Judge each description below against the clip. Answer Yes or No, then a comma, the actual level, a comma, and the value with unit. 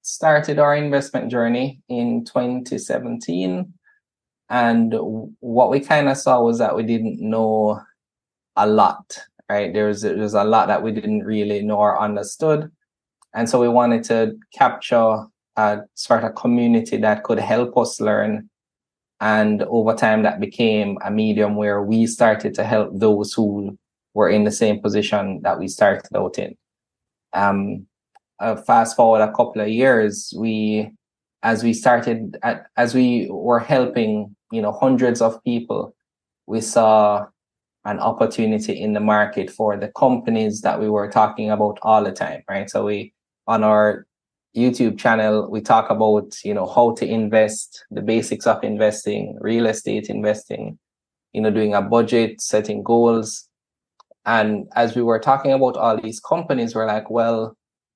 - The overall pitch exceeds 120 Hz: No, low, 110 Hz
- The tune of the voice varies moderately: No, narrow, 2.0 semitones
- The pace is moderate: Yes, average, 160 wpm